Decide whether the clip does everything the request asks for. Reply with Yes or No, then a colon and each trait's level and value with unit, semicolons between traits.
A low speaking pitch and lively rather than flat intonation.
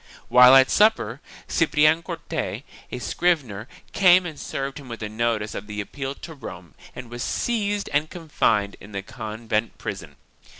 Yes: low, 130 Hz; wide, 7.0 semitones